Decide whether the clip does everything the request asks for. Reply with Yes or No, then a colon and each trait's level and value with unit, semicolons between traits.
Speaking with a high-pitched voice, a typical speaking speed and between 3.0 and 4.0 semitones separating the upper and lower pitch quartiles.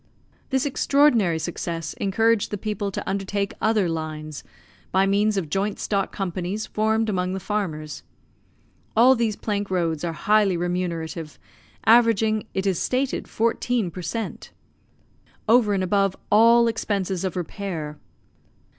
No: high, 200 Hz; slow, 130 wpm; average, 3.7 semitones